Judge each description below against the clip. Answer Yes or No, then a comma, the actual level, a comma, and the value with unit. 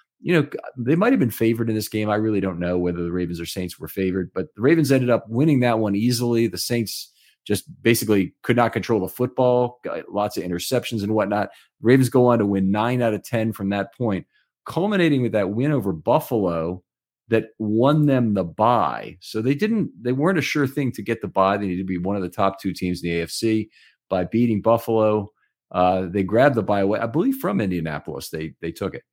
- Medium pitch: No, low, 110 Hz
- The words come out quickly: Yes, fast, 225 wpm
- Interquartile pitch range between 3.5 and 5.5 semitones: Yes, average, 4.2 semitones